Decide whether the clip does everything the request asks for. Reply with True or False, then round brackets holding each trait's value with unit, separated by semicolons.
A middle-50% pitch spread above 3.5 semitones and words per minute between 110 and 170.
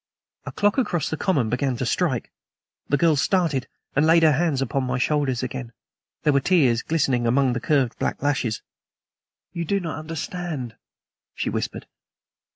True (4.4 semitones; 160 wpm)